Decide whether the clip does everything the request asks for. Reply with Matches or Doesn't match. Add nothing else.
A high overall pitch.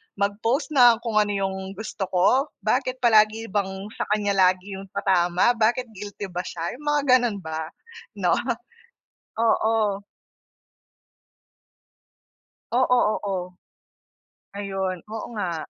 Matches